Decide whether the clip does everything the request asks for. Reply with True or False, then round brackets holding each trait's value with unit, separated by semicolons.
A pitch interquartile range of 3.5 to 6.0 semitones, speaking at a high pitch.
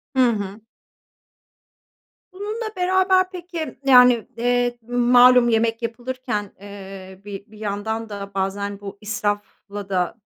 True (3.8 semitones; 225 Hz)